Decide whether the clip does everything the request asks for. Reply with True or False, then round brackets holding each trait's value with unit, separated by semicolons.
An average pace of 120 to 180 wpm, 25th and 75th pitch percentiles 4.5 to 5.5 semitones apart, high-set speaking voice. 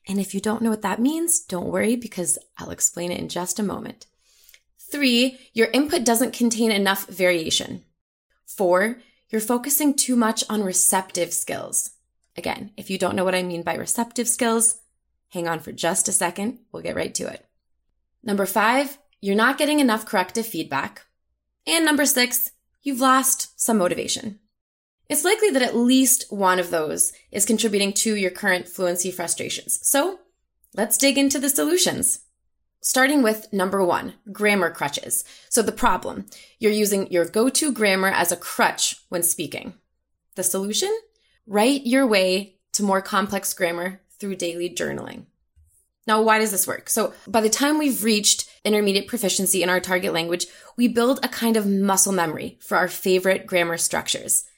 True (165 wpm; 4.8 semitones; 210 Hz)